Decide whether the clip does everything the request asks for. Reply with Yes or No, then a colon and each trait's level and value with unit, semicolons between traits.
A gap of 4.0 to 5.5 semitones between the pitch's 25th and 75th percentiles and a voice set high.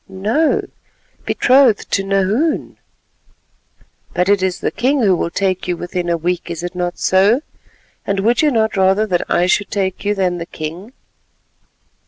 No: average, 3.4 semitones; high, 195 Hz